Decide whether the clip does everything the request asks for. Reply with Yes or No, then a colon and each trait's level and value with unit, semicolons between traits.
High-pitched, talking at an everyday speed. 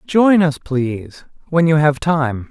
No: medium, 155 Hz; average, 170 wpm